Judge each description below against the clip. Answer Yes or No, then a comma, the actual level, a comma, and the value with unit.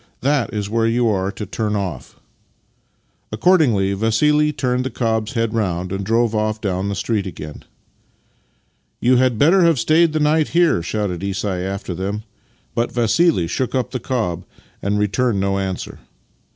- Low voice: Yes, low, 110 Hz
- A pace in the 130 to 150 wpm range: No, average, 165 wpm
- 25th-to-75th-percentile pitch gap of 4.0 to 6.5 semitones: Yes, average, 4.6 semitones